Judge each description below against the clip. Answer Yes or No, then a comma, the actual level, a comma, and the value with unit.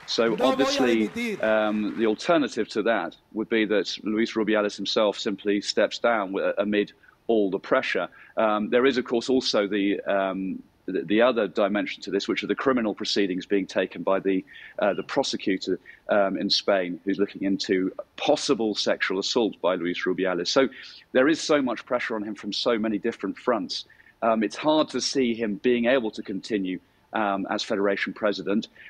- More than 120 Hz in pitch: No, low, 105 Hz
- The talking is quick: No, average, 175 wpm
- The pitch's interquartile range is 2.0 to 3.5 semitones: Yes, average, 2.7 semitones